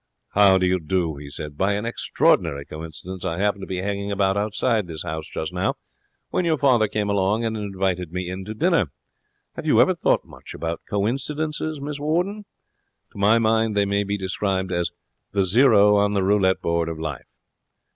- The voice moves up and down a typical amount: Yes, average, 3.2 semitones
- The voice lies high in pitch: No, low, 100 Hz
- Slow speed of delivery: No, average, 190 wpm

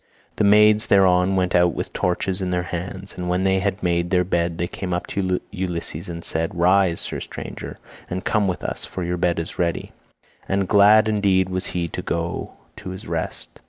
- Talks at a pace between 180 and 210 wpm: Yes, average, 200 wpm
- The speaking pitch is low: Yes, very low, 90 Hz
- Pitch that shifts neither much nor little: No, narrow, 1.7 semitones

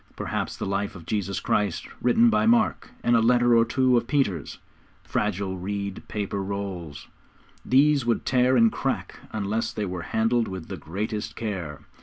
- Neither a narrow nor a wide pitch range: Yes, average, 3.8 semitones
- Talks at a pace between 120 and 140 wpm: No, average, 165 wpm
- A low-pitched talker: Yes, low, 105 Hz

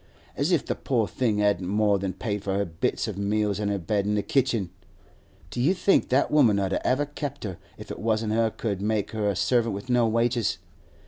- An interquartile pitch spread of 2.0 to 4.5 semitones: Yes, average, 3.2 semitones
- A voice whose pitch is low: Yes, low, 110 Hz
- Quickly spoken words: Yes, fast, 230 wpm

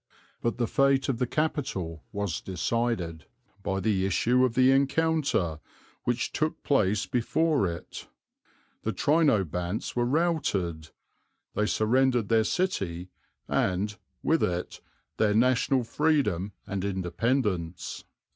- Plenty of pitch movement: Yes, wide, 6.3 semitones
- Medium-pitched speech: No, low, 110 Hz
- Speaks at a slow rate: Yes, slow, 115 wpm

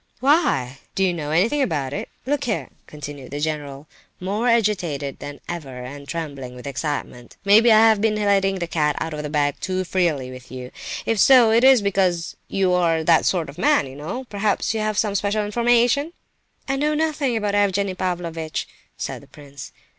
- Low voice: No, medium, 180 Hz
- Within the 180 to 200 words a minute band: Yes, average, 185 wpm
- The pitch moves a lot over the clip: Yes, wide, 6.8 semitones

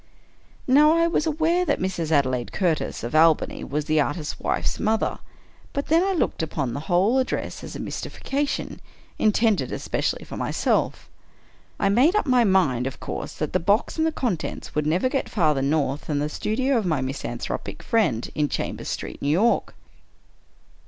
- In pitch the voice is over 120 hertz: Yes, high, 190 Hz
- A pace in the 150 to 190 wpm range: Yes, average, 170 wpm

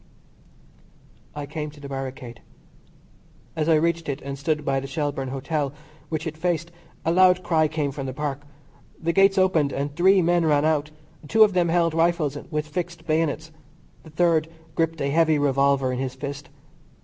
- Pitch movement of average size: Yes, average, 3.0 semitones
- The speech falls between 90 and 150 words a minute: No, average, 175 wpm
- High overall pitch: No, medium, 155 Hz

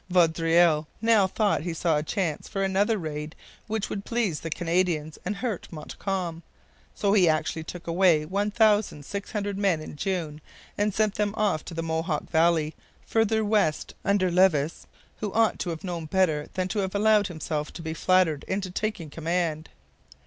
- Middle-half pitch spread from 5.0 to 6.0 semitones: No, average, 4.1 semitones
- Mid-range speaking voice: Yes, medium, 180 Hz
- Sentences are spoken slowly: No, average, 165 wpm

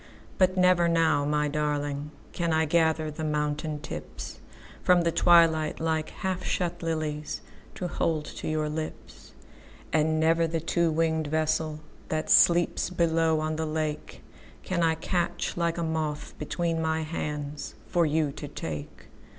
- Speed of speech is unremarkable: No, slow, 125 wpm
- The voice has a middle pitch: Yes, medium, 160 Hz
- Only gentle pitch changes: Yes, narrow, 1.7 semitones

